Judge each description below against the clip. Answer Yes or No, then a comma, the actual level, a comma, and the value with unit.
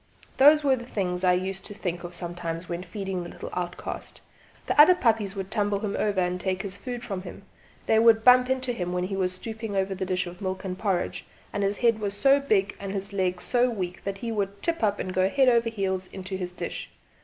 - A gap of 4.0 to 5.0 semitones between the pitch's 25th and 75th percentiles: No, average, 3.4 semitones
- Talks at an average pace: No, fast, 235 wpm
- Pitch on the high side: Yes, high, 195 Hz